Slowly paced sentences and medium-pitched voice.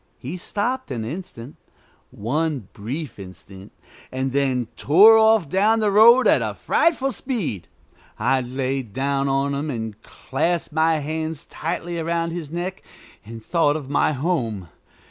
No: average, 145 wpm; medium, 150 Hz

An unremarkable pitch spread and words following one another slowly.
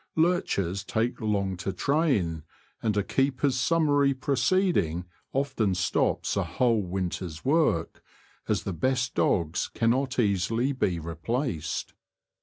No: wide, 7.1 semitones; slow, 115 wpm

